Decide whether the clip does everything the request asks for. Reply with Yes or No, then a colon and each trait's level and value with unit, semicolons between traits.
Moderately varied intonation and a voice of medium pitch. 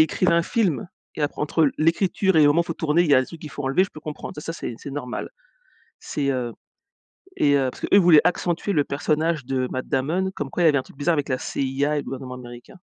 Yes: average, 3.7 semitones; medium, 150 Hz